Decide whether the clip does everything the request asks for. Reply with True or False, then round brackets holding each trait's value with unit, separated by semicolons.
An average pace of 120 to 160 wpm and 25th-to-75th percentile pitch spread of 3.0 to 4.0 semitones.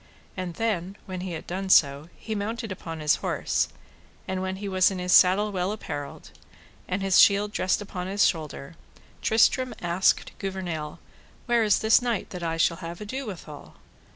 False (175 wpm; 3.4 semitones)